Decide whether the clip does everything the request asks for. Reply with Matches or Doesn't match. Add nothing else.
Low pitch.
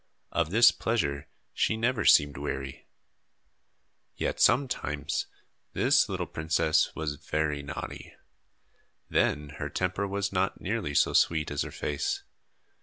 Matches